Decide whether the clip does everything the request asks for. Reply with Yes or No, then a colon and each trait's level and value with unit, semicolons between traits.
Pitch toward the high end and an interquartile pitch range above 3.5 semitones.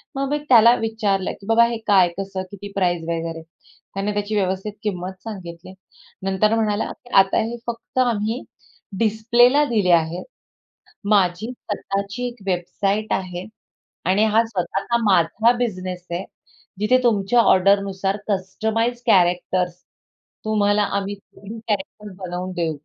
No: high, 200 Hz; average, 3.2 semitones